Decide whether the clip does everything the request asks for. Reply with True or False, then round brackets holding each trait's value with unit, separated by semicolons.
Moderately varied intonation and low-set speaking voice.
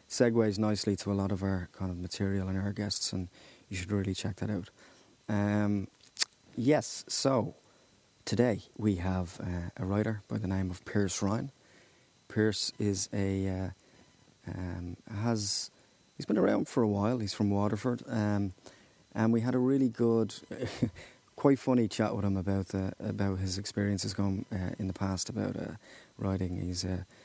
False (2.1 semitones; 100 Hz)